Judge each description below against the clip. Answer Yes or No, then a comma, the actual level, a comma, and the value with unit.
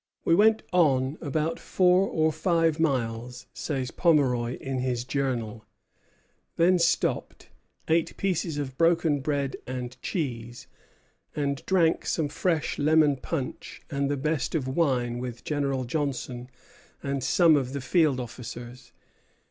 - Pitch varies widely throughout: No, average, 4.3 semitones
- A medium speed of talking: No, slow, 130 wpm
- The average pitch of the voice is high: No, medium, 140 Hz